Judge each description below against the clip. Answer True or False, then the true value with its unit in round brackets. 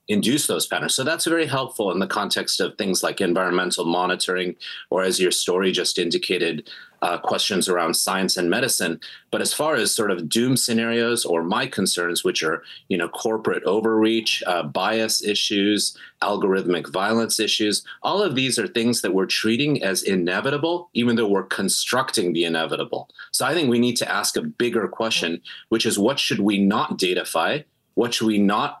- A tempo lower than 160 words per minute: False (180 wpm)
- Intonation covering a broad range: False (4.2 semitones)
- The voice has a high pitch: False (110 Hz)